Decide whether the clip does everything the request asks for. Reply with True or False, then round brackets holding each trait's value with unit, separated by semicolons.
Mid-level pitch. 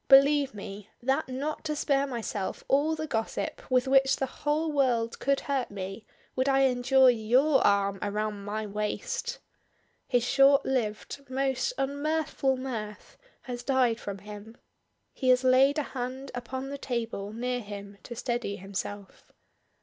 False (255 Hz)